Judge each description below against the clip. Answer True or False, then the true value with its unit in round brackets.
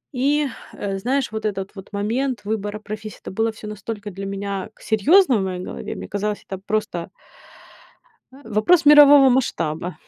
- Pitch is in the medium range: False (215 Hz)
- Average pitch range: True (4.3 semitones)